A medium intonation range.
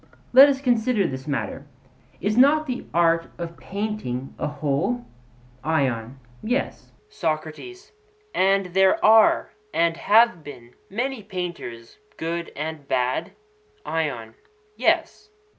No: wide, 7.3 semitones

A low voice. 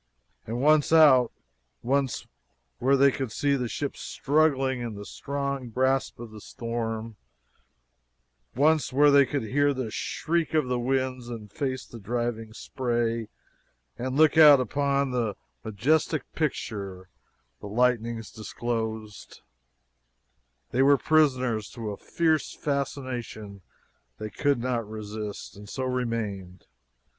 Yes: low, 125 Hz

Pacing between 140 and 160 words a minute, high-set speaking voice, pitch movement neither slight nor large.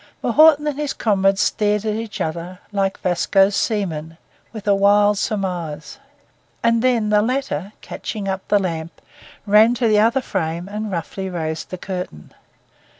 Yes: average, 150 wpm; high, 200 Hz; average, 3.4 semitones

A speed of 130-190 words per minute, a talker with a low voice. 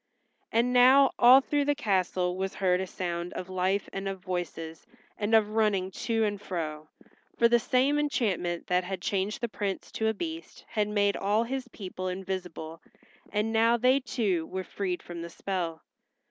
No: average, 175 wpm; high, 200 Hz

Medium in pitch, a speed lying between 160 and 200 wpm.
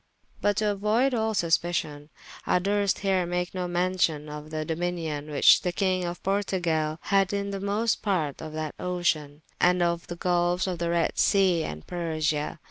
Yes: medium, 175 Hz; average, 175 wpm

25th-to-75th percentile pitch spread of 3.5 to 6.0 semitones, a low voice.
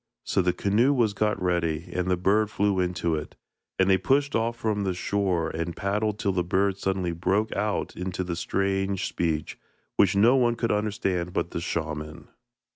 No: average, 3.1 semitones; very low, 95 Hz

